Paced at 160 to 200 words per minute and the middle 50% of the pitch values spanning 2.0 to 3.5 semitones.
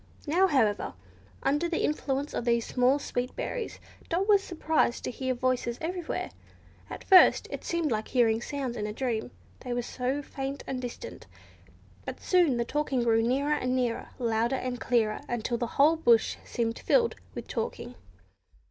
No: average, 165 wpm; average, 4.0 semitones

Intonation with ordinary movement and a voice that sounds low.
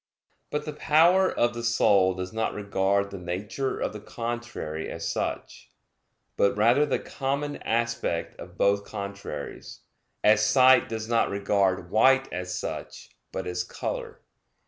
Yes: average, 4.3 semitones; low, 110 Hz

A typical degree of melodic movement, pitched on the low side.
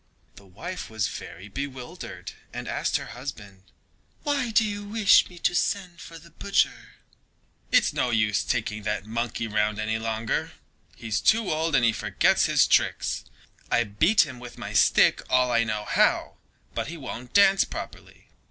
No: wide, 8.3 semitones; low, 125 Hz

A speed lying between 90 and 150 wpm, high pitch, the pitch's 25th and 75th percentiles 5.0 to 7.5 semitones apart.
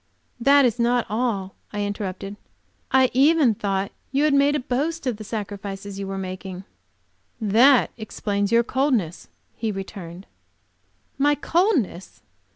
Yes: slow, 135 wpm; high, 220 Hz; average, 5.3 semitones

